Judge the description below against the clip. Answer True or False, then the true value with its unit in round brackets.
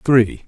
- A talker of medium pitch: False (120 Hz)